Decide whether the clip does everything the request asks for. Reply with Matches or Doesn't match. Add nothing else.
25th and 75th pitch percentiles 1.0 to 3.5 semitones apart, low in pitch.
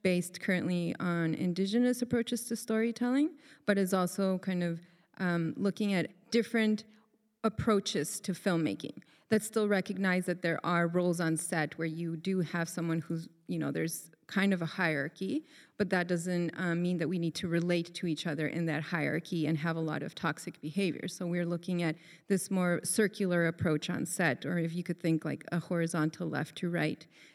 Doesn't match